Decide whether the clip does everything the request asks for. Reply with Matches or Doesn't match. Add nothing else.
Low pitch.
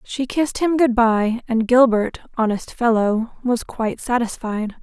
Doesn't match